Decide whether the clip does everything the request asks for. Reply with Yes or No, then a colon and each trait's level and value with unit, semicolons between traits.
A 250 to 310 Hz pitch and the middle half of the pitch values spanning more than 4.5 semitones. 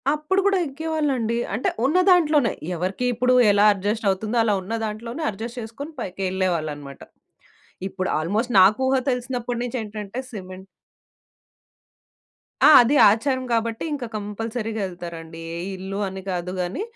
No: high, 220 Hz; average, 5.0 semitones